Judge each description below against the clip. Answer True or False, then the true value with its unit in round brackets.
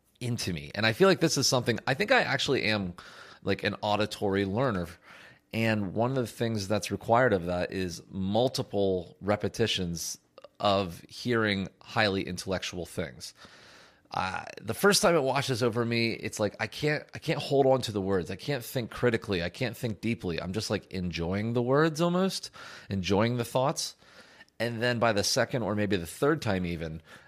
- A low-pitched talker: True (110 Hz)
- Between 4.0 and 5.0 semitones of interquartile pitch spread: True (4.4 semitones)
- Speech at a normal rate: True (185 wpm)